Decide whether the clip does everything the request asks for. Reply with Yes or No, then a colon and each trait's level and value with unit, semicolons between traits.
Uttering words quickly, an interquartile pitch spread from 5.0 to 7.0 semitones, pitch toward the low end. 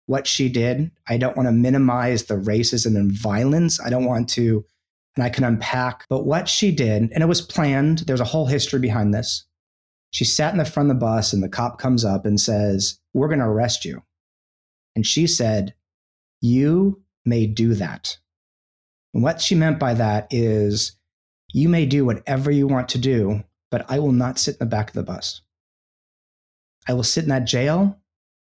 No: average, 195 wpm; average, 5.3 semitones; low, 120 Hz